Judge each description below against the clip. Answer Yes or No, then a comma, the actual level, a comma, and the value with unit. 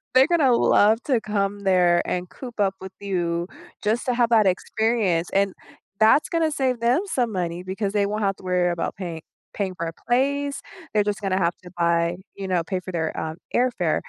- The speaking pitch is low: No, high, 200 Hz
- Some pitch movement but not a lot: Yes, average, 4.8 semitones